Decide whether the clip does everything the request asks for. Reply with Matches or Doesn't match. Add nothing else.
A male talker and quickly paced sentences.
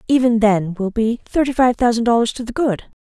Doesn't match